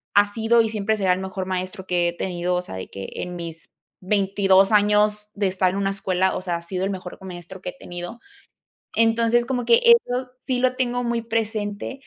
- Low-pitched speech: No, high, 200 Hz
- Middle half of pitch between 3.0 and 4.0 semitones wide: Yes, average, 3.6 semitones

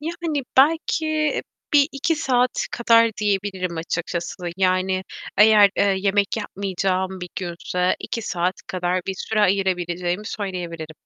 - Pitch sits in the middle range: No, high, 195 Hz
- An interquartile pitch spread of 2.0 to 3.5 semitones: No, average, 4.2 semitones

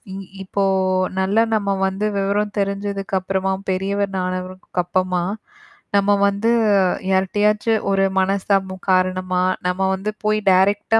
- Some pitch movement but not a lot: No, narrow, 1.4 semitones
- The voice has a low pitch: No, high, 195 Hz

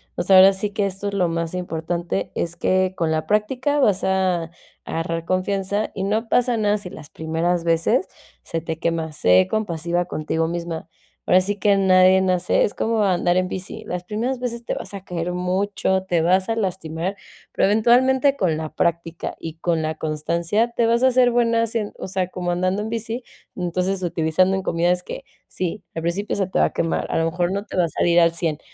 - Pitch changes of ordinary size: Yes, average, 3.5 semitones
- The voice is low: No, medium, 185 Hz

